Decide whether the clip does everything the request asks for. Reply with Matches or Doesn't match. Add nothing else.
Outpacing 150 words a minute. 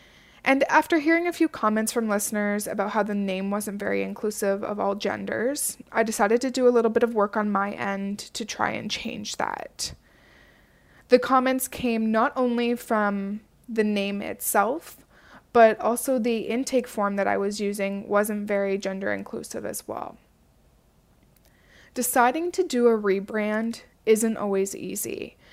Matches